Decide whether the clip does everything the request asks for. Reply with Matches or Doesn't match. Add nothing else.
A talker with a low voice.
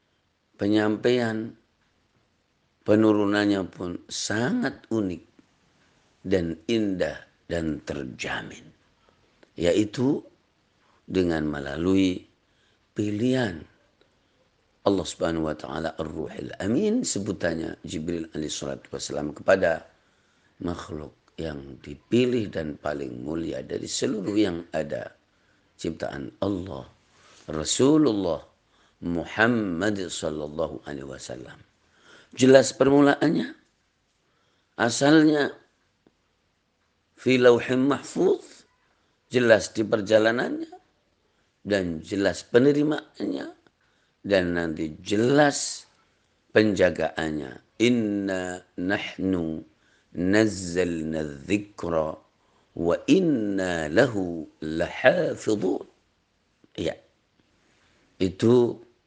Matches